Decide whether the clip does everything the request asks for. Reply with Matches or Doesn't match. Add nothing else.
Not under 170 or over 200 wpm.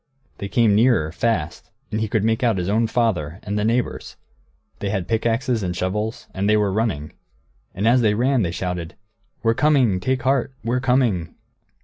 Matches